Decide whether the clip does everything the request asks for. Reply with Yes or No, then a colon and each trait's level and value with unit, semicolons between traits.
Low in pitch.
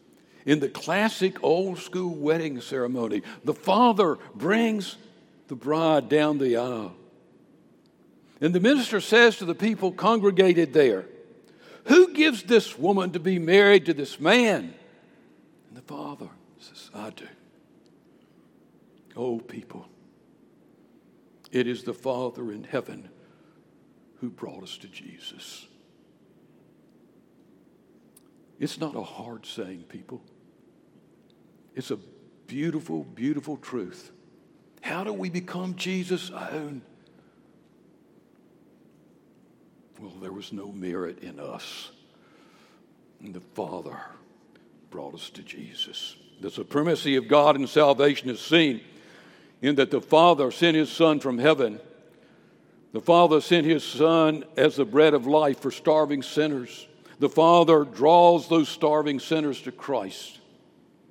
No: medium, 155 Hz